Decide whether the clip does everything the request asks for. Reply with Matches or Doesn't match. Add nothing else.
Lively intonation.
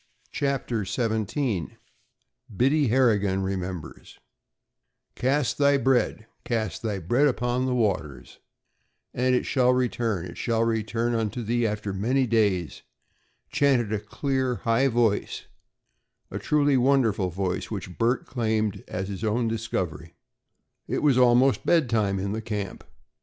Doesn't match